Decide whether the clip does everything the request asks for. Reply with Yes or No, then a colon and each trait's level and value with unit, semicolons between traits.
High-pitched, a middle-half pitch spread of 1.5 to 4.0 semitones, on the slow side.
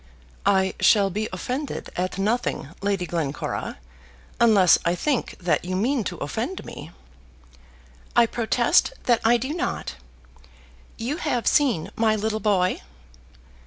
No: high, 215 Hz; average, 4.6 semitones; slow, 125 wpm